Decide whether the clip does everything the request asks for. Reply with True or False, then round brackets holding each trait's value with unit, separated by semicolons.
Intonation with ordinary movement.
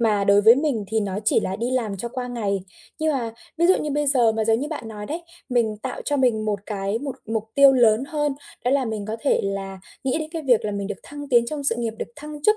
True (4.8 semitones)